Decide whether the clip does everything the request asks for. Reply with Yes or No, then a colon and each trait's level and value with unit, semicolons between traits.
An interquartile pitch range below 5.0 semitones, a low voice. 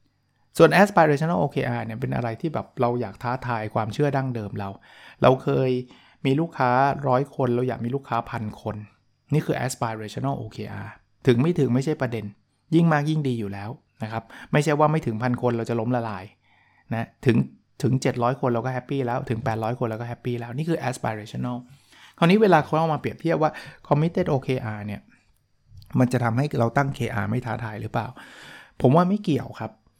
Yes: average, 3.7 semitones; low, 125 Hz